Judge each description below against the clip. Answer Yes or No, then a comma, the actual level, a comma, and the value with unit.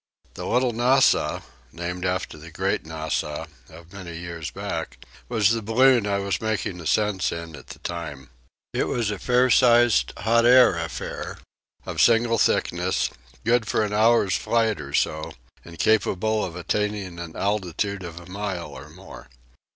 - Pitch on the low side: Yes, low, 100 Hz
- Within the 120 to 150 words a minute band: No, average, 160 wpm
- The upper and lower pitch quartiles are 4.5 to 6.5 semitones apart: Yes, average, 4.9 semitones